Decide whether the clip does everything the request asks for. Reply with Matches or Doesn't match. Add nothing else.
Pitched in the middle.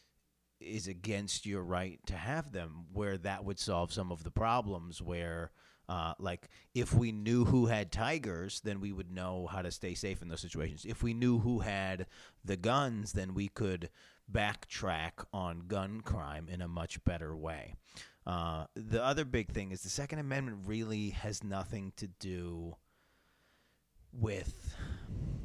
Doesn't match